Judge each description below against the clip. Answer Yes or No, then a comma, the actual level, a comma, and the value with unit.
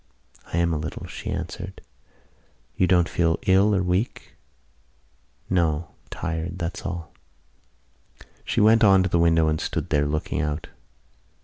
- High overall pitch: No, very low, 85 Hz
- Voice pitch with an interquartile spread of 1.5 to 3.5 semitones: Yes, average, 2.7 semitones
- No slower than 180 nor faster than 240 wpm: No, average, 140 wpm